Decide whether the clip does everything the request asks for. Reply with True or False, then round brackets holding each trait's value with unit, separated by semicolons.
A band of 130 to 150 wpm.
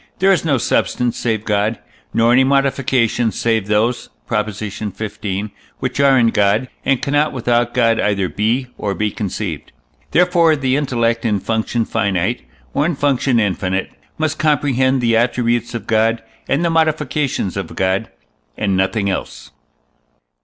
True (145 wpm)